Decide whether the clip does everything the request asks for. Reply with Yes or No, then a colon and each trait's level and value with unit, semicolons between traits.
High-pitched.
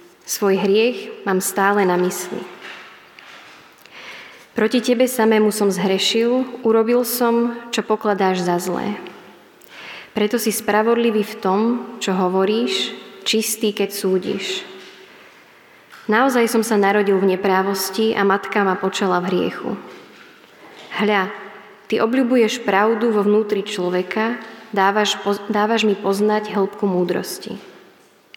Yes: high, 210 Hz